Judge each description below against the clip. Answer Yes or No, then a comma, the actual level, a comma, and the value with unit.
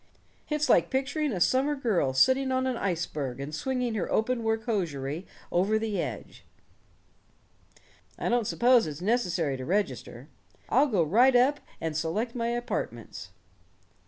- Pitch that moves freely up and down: Yes, wide, 7.0 semitones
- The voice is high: Yes, high, 225 Hz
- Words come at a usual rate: Yes, average, 145 wpm